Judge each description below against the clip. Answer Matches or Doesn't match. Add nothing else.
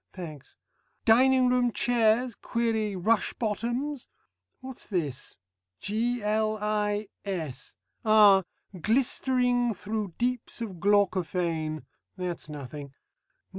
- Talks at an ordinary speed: Doesn't match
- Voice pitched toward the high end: Matches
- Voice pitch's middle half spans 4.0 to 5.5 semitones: Matches